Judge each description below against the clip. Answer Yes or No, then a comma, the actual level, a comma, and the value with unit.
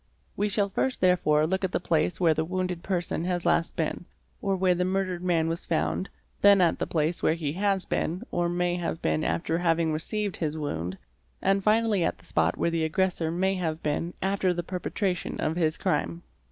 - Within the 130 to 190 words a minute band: No, fast, 205 wpm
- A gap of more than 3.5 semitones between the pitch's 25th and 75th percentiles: No, average, 2.7 semitones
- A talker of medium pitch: Yes, medium, 175 Hz